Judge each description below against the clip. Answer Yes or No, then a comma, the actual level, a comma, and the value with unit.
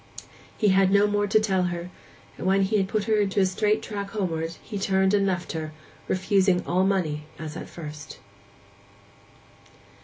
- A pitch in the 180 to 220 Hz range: Yes, high, 190 Hz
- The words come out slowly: No, average, 165 wpm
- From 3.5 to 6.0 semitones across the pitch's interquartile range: No, narrow, 2.4 semitones